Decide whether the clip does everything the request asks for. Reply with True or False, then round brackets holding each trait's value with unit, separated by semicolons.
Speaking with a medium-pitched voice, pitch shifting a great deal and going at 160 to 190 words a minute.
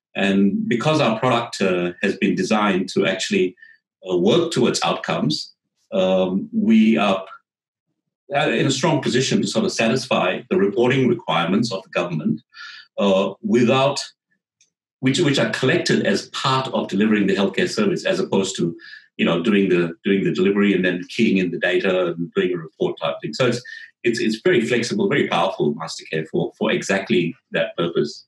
False (100 Hz; 6.1 semitones; 170 wpm)